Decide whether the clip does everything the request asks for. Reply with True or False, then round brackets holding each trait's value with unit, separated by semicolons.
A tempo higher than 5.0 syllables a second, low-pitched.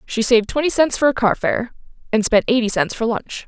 False (5.5 syllables/s; 235 Hz)